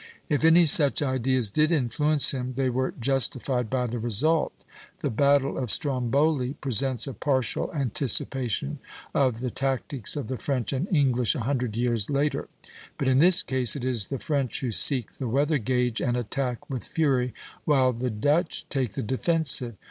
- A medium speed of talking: Yes, average, 170 wpm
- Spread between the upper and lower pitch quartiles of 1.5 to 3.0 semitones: Yes, average, 2.7 semitones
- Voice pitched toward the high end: No, low, 130 Hz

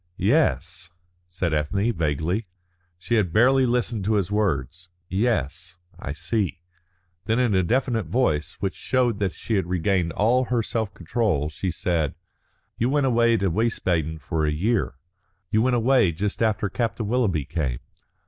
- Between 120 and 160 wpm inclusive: Yes, average, 155 wpm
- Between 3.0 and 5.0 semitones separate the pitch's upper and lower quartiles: No, wide, 5.6 semitones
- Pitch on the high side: No, low, 100 Hz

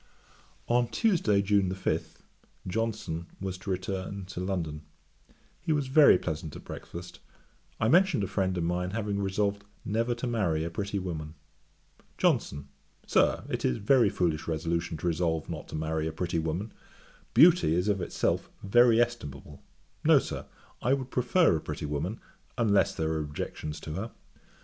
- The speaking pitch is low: Yes, very low, 95 Hz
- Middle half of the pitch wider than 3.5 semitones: Yes, wide, 5.6 semitones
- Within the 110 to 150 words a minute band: No, average, 160 wpm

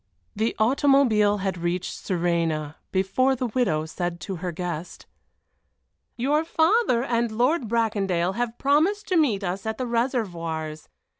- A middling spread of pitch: No, wide, 6.4 semitones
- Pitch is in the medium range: No, high, 215 Hz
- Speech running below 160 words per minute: Yes, average, 140 wpm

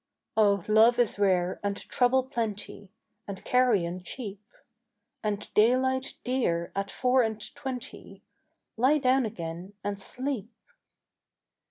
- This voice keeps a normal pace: No, slow, 115 wpm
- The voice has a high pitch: Yes, high, 220 Hz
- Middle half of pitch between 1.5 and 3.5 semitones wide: No, average, 4.2 semitones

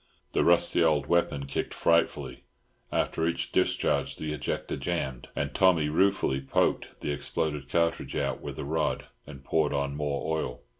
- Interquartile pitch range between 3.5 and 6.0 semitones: No, average, 2.8 semitones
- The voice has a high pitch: No, very low, 75 Hz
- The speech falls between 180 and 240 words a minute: No, average, 155 wpm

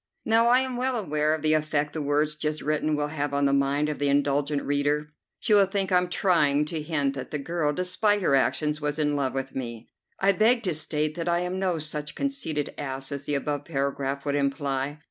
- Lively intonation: No, average, 3.5 semitones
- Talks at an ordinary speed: No, fast, 220 wpm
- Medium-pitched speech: Yes, medium, 150 Hz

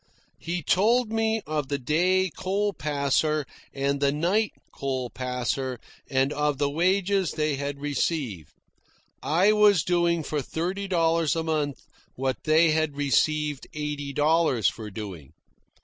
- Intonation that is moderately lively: Yes, average, 3.9 semitones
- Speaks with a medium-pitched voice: Yes, medium, 150 Hz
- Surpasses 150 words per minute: No, slow, 135 wpm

